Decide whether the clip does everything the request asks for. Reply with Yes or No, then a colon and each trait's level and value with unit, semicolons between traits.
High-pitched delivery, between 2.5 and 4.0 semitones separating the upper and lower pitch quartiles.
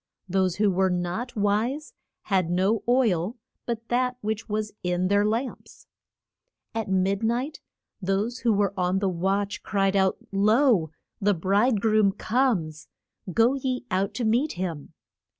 Yes: high, 205 Hz; average, 3.7 semitones